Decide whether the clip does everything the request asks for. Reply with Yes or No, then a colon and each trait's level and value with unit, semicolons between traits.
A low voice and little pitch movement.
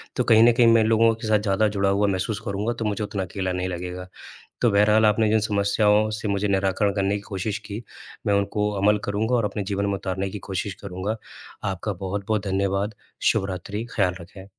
Yes: low, 100 Hz; narrow, 1.8 semitones